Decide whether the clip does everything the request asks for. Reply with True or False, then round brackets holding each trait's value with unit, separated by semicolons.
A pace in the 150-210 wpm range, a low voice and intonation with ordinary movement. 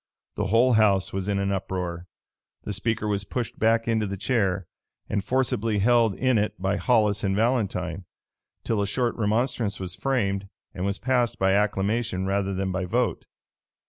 True (170 wpm; 105 Hz; 3.1 semitones)